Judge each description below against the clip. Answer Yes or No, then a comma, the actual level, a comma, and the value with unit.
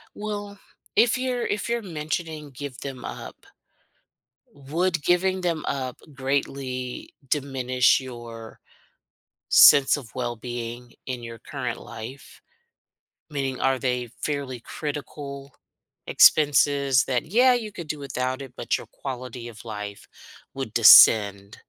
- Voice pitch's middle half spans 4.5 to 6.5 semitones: No, average, 3.7 semitones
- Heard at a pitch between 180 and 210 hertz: No, low, 135 Hz